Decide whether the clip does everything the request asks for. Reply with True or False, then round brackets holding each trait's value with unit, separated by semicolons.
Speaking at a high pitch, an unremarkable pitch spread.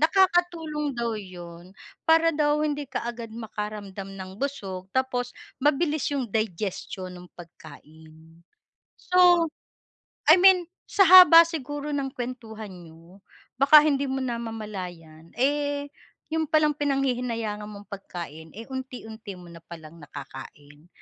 False (235 Hz; 8.1 semitones)